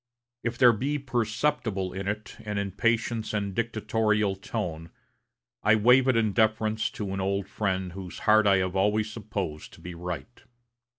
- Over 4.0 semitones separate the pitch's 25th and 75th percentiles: No, narrow, 2.5 semitones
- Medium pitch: No, low, 105 Hz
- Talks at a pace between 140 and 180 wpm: Yes, average, 160 wpm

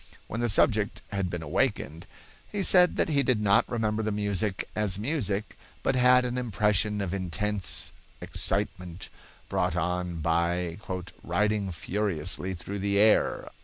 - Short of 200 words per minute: Yes, average, 140 wpm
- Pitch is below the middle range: Yes, low, 100 Hz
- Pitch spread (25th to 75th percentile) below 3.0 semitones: No, average, 3.3 semitones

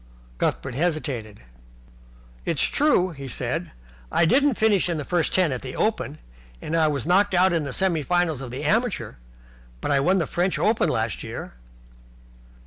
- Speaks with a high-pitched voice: No, medium, 165 Hz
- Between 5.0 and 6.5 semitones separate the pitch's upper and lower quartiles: Yes, average, 5.3 semitones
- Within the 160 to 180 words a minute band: Yes, average, 170 wpm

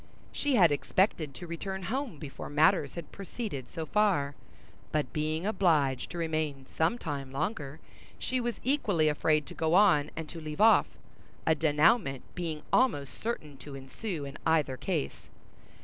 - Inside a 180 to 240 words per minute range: No, average, 155 wpm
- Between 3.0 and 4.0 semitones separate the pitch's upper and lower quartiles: No, average, 5.0 semitones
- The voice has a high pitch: No, medium, 160 Hz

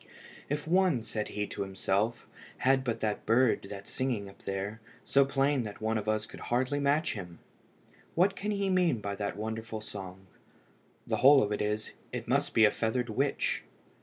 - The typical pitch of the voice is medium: No, low, 110 Hz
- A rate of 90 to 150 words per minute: No, average, 185 wpm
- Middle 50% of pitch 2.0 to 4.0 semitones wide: No, average, 4.8 semitones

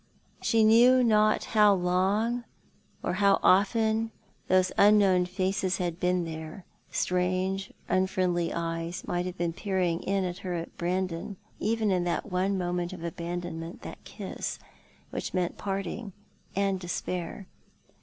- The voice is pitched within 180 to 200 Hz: Yes, medium, 185 Hz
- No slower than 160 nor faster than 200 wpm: No, slow, 135 wpm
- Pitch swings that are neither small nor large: No, narrow, 2.2 semitones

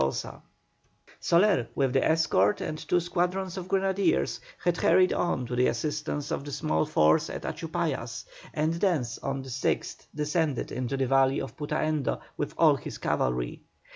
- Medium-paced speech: Yes, average, 155 wpm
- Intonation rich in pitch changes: No, average, 5.0 semitones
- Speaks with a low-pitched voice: No, medium, 150 Hz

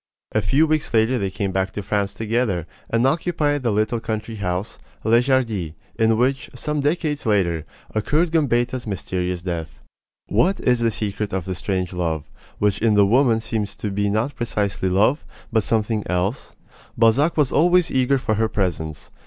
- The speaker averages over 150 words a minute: Yes, average, 170 wpm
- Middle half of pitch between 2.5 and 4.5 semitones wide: No, average, 4.9 semitones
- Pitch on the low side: Yes, low, 110 Hz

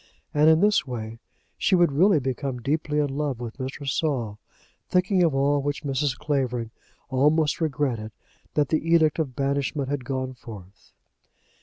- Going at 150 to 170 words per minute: Yes, average, 155 wpm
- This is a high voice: No, medium, 140 Hz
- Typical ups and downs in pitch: Yes, average, 3.0 semitones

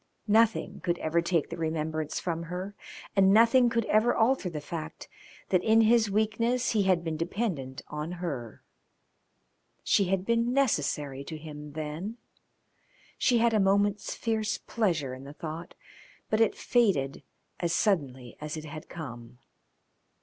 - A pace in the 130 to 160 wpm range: Yes, average, 150 wpm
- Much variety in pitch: Yes, wide, 6.1 semitones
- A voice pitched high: No, medium, 175 Hz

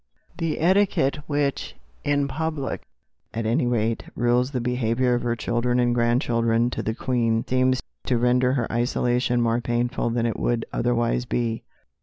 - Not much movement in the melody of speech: Yes, narrow, 1.6 semitones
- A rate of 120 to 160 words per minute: Yes, average, 155 wpm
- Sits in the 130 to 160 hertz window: No, low, 120 Hz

